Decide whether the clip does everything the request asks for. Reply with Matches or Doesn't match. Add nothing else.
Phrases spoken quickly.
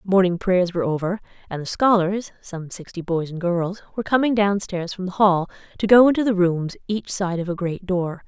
Matches